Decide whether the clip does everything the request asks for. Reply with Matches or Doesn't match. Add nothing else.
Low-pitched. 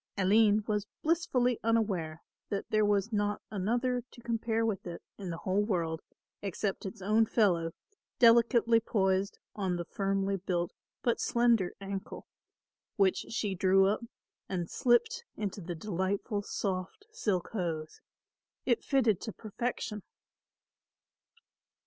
Doesn't match